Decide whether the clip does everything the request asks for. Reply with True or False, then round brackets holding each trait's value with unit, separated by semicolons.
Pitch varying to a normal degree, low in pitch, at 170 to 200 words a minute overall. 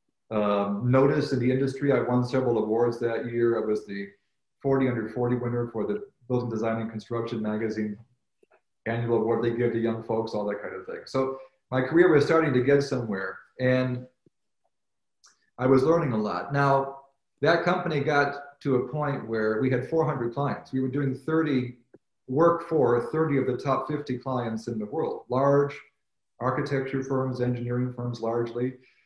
True (3.0 semitones; 125 Hz; 175 wpm)